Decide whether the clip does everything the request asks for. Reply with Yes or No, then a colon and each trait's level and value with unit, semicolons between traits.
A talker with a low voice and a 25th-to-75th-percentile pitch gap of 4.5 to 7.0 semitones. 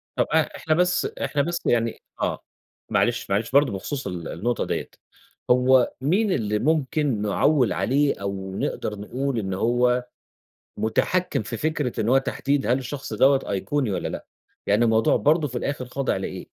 Yes: low, 125 Hz; average, 4.8 semitones